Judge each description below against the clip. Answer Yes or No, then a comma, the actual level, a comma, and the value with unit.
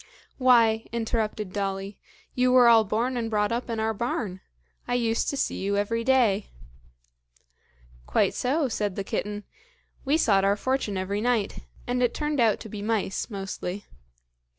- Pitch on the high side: Yes, high, 220 Hz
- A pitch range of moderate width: Yes, average, 3.3 semitones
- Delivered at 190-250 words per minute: No, average, 160 wpm